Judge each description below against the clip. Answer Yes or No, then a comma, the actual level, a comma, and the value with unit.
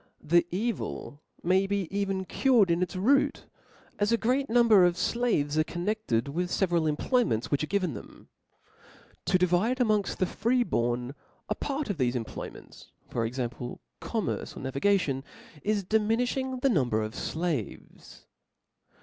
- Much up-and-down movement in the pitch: Yes, wide, 7.5 semitones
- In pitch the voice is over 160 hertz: Yes, medium, 185 Hz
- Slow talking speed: No, average, 155 wpm